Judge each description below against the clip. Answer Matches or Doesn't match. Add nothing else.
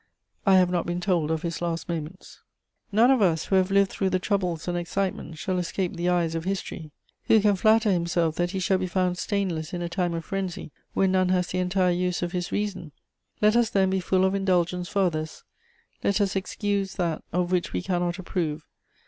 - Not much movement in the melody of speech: Matches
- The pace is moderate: Doesn't match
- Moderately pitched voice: Matches